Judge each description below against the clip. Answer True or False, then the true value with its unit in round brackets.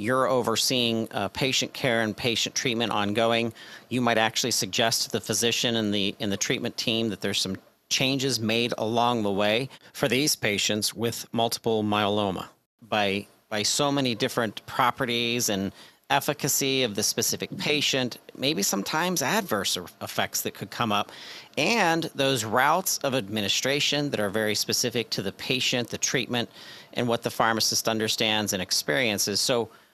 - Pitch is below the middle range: True (115 Hz)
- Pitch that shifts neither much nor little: True (3.3 semitones)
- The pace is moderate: True (155 wpm)